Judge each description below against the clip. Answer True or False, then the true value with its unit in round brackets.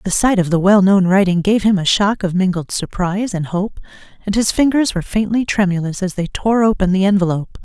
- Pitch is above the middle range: True (195 Hz)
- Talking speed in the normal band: False (210 wpm)